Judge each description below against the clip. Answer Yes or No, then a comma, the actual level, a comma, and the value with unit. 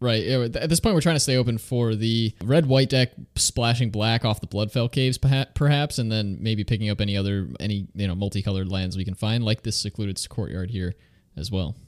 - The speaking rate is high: Yes, fast, 215 wpm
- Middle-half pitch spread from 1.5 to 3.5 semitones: No, average, 3.9 semitones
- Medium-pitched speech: No, low, 110 Hz